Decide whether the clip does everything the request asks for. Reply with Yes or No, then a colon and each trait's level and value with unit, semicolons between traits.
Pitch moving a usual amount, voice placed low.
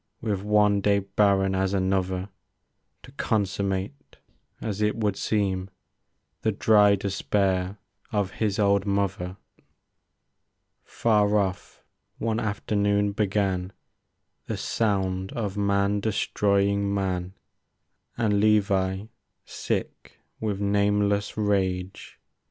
No: narrow, 1.3 semitones; low, 100 Hz